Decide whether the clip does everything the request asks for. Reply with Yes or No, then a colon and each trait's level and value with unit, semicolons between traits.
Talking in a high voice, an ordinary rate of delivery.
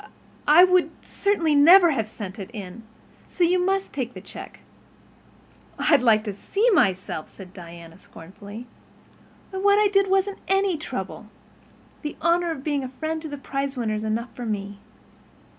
Yes: very high, 285 Hz; average, 160 wpm